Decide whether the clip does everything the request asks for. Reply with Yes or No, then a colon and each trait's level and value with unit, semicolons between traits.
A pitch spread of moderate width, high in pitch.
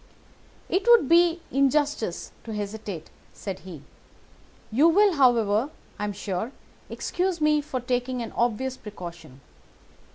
No: wide, 6.5 semitones; high, 245 Hz